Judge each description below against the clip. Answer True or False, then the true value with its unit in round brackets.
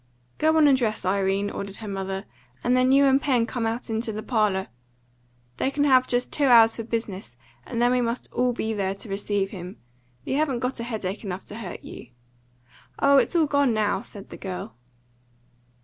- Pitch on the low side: False (230 Hz)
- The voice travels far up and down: False (4.3 semitones)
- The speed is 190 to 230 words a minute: True (195 wpm)